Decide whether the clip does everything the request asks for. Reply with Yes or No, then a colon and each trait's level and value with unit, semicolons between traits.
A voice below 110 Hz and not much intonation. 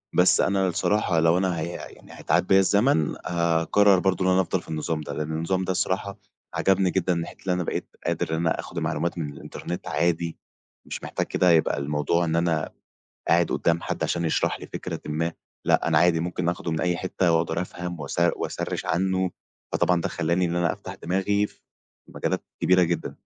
Yes: very low, 85 Hz; narrow, 2.1 semitones